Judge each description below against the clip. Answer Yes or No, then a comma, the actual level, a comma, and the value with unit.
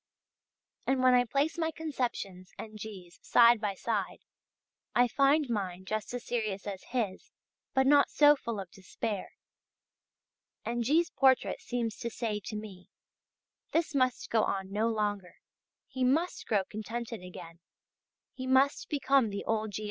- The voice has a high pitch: Yes, high, 230 Hz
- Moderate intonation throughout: Yes, average, 4.4 semitones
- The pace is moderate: Yes, average, 150 wpm